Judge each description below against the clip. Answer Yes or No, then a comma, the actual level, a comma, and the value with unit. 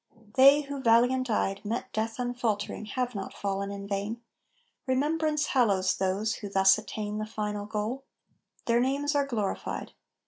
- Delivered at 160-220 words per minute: No, average, 145 wpm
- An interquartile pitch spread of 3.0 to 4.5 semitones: Yes, average, 4.1 semitones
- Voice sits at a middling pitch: No, high, 225 Hz